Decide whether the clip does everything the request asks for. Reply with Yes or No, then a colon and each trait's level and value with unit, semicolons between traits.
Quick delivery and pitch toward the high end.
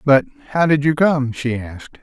No: fast, 210 wpm; medium, 145 Hz